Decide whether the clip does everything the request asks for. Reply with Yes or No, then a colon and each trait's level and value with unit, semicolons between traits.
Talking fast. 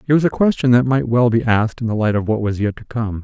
Yes: fast, 335 wpm